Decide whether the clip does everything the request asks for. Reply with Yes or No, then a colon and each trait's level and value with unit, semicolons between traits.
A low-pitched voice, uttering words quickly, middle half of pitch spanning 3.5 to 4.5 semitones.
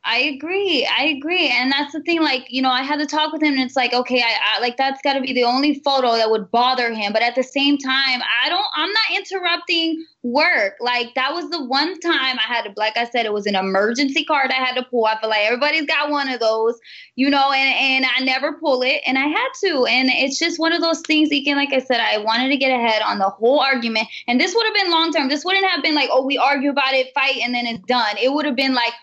No: very high, 270 Hz; fast, 280 wpm; average, 3.9 semitones